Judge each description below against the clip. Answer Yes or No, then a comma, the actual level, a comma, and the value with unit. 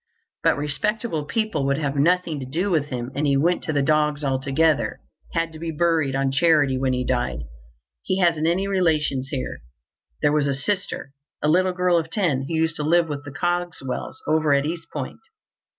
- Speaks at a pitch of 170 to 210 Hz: No, medium, 155 Hz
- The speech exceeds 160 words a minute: Yes, average, 190 wpm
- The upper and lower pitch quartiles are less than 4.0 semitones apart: Yes, average, 3.6 semitones